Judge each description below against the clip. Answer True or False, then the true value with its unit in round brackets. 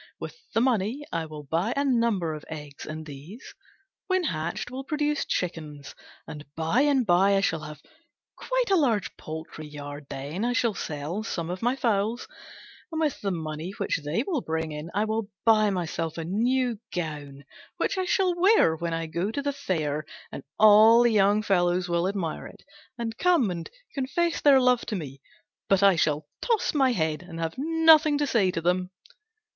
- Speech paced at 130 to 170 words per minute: False (185 wpm)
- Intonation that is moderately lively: False (7.7 semitones)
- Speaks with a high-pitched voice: True (195 Hz)